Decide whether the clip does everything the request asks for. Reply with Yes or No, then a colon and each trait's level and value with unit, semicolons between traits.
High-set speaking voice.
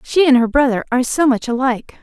Yes: very high, 255 Hz